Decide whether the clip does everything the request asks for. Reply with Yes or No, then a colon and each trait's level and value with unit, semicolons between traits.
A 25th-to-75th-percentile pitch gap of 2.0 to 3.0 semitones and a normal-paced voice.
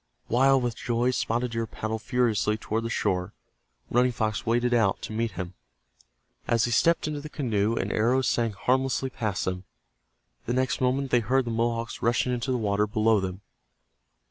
Yes: narrow, 2.6 semitones; average, 175 wpm